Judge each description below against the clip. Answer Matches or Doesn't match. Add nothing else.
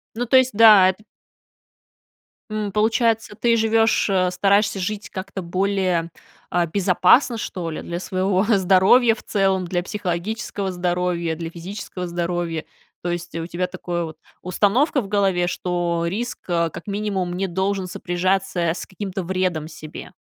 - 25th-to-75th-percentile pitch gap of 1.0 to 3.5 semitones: Matches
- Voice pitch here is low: Doesn't match